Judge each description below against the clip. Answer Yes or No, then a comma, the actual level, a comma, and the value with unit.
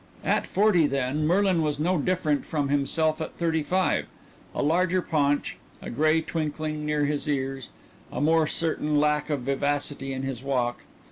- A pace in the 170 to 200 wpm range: No, average, 160 wpm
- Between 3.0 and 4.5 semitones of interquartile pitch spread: No, narrow, 2.4 semitones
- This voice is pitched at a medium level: Yes, medium, 150 Hz